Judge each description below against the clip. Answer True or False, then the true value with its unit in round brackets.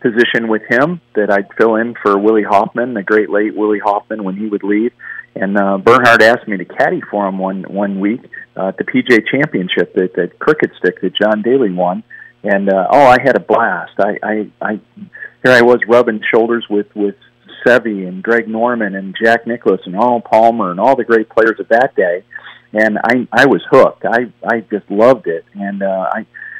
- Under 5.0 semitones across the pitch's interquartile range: True (2.7 semitones)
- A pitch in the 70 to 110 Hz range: True (105 Hz)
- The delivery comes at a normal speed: False (210 wpm)